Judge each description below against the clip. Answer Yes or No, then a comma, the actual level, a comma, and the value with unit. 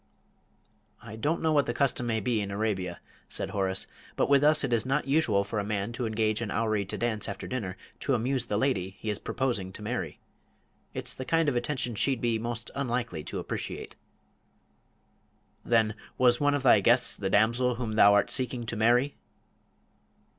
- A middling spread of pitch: Yes, average, 3.4 semitones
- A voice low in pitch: Yes, low, 115 Hz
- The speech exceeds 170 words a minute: Yes, average, 190 wpm